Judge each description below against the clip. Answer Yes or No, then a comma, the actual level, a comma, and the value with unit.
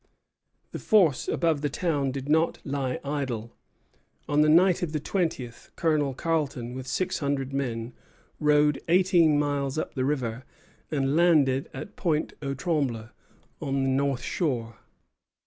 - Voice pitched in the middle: Yes, medium, 145 Hz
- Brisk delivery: No, average, 145 wpm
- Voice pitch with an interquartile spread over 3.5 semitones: No, average, 3.2 semitones